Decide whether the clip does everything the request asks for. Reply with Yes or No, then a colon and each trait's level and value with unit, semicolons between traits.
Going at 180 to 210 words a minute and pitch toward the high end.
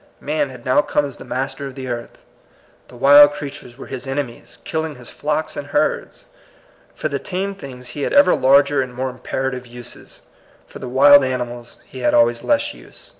No: average, 200 wpm; low, 135 Hz